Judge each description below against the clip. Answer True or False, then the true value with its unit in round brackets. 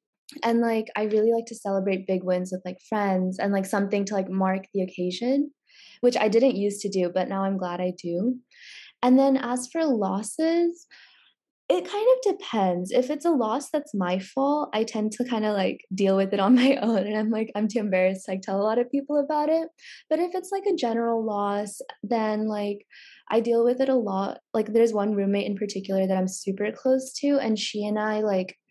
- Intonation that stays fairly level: False (4.8 semitones)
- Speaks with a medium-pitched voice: False (215 Hz)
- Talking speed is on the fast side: True (220 wpm)